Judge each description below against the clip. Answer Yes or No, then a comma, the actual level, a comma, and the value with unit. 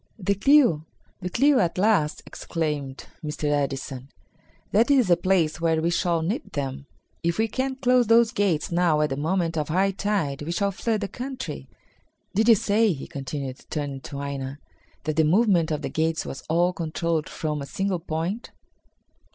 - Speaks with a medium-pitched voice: Yes, medium, 170 Hz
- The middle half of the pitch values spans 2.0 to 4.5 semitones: No, average, 5.2 semitones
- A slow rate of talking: No, average, 175 wpm